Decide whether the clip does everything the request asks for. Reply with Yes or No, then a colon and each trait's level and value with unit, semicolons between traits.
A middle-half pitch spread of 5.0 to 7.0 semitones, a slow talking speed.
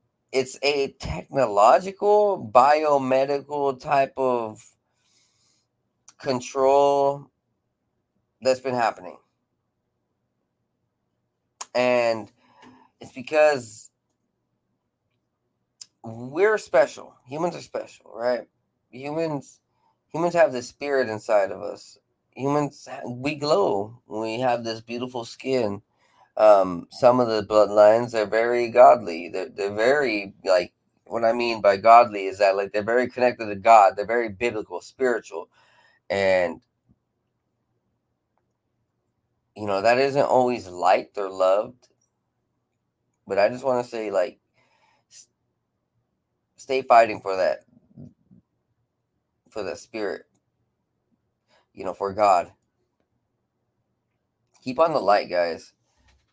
No: average, 3.9 semitones; slow, 105 wpm